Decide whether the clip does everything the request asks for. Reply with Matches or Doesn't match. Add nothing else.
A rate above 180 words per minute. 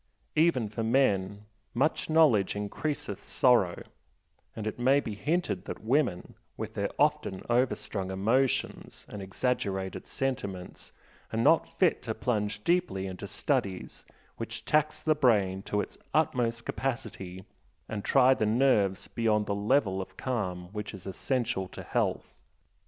Doesn't match